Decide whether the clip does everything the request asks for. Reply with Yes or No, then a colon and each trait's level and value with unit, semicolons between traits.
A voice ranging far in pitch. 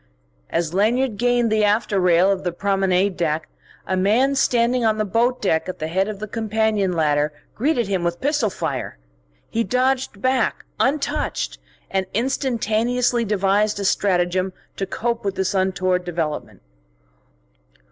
No: average, 4.2 semitones